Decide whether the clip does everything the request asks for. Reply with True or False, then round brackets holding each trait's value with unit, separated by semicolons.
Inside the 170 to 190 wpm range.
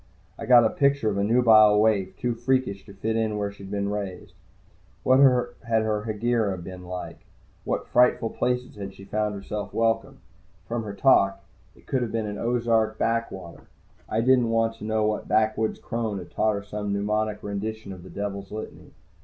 True (185 wpm)